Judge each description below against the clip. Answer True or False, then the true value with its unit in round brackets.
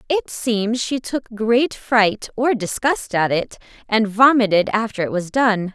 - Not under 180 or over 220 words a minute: False (165 wpm)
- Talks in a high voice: True (225 Hz)